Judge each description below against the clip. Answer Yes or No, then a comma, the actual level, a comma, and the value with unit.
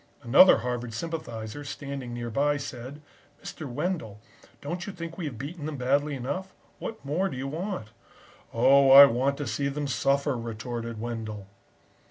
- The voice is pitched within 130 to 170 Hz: Yes, medium, 140 Hz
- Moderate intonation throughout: Yes, average, 3.8 semitones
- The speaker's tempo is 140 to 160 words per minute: Yes, average, 155 wpm